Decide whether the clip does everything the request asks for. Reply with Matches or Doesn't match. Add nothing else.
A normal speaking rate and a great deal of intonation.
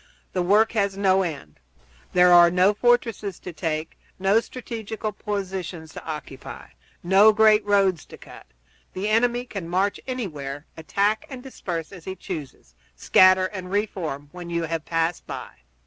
Doesn't match